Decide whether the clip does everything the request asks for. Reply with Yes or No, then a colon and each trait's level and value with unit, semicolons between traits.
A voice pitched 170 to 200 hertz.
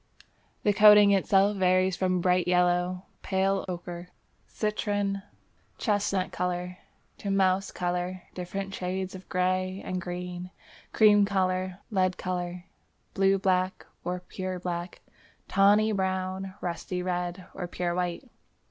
Yes: medium, 185 Hz